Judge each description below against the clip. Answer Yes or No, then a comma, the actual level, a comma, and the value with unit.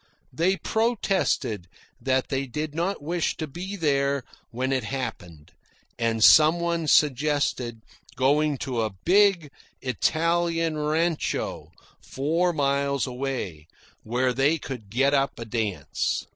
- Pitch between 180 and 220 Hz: No, medium, 140 Hz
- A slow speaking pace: Yes, slow, 120 wpm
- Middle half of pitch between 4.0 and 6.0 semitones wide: Yes, average, 4.7 semitones